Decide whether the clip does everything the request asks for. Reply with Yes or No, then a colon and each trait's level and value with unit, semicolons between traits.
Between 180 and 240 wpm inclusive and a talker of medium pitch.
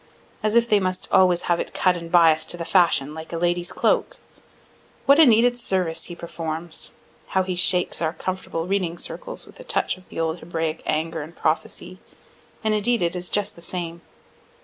Yes: average, 195 wpm; medium, 175 Hz